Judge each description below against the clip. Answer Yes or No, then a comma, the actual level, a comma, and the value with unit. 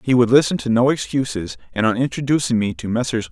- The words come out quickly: Yes, fast, 215 wpm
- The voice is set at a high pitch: No, low, 120 Hz